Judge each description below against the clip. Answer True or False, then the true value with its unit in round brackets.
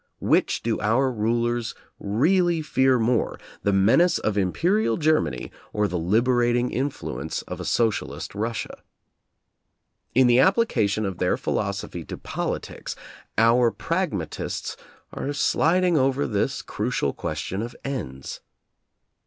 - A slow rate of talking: True (120 wpm)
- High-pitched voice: False (120 Hz)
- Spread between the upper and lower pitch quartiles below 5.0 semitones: False (5.3 semitones)